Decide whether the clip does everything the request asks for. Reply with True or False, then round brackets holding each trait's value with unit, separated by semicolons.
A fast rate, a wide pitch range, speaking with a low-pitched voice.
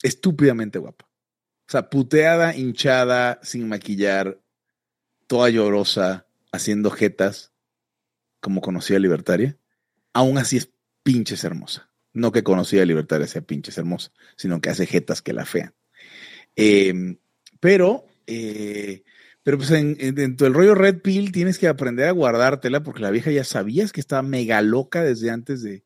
False (145 wpm; 5.9 semitones; 120 Hz)